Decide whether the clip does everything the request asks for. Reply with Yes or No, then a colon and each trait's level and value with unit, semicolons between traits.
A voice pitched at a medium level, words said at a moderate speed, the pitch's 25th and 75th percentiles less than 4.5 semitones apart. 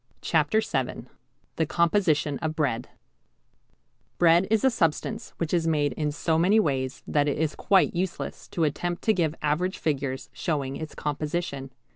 Yes: medium, 160 Hz; average, 155 wpm; average, 3.2 semitones